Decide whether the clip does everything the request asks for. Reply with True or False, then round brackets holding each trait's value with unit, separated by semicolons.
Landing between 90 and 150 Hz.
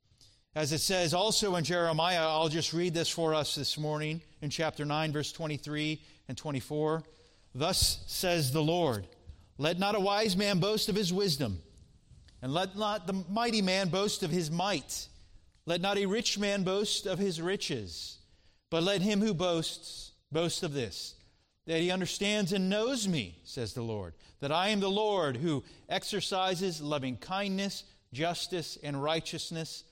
False (165 Hz)